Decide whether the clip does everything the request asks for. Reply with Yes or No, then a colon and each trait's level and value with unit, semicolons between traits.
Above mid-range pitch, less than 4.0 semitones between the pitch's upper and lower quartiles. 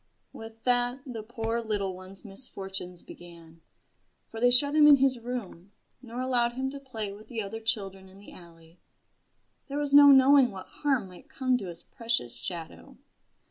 No: high, 225 Hz; average, 5.1 semitones